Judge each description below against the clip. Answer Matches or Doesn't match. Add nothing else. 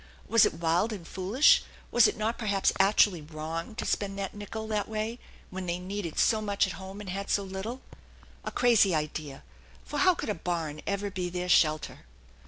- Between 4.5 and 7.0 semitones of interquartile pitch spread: Doesn't match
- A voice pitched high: Matches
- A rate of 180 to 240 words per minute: Matches